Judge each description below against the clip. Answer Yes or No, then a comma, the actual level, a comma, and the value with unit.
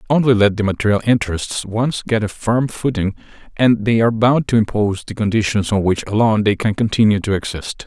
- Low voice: Yes, low, 110 Hz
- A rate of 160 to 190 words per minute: No, average, 200 wpm